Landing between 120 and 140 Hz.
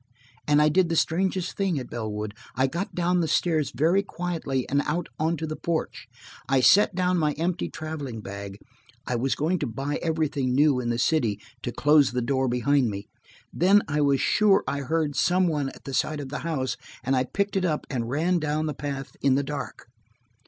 No: medium, 150 Hz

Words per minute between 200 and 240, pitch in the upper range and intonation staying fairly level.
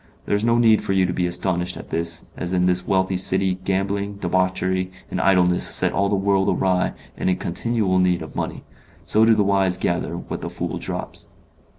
No: fast, 205 wpm; very low, 95 Hz; narrow, 1.6 semitones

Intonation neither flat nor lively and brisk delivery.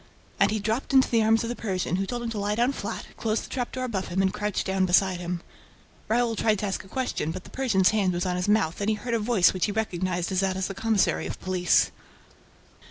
Yes: average, 3.3 semitones; fast, 260 wpm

